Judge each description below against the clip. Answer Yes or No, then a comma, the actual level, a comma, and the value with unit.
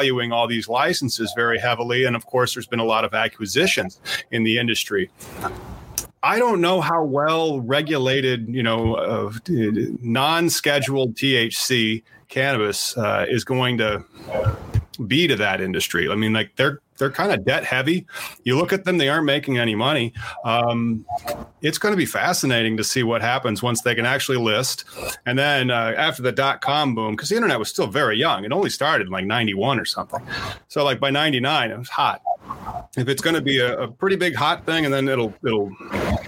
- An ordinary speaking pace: Yes, average, 190 wpm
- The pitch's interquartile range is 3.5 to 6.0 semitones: Yes, average, 3.9 semitones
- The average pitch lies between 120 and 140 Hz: Yes, low, 125 Hz